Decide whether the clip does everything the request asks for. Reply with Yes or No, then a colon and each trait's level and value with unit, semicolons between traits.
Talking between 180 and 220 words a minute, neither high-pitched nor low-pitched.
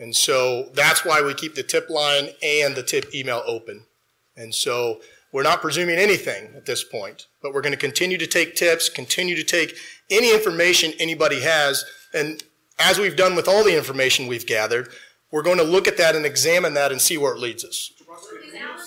Yes: average, 200 wpm; medium, 165 Hz